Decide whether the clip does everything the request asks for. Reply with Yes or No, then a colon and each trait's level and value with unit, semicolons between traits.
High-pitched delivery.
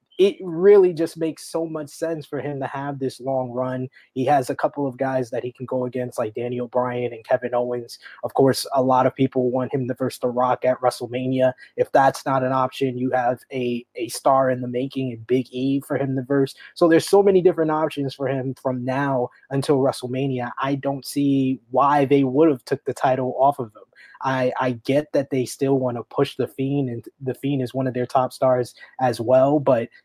No: low, 130 Hz